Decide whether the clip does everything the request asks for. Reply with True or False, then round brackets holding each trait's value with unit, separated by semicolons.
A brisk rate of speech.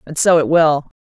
True (235 wpm)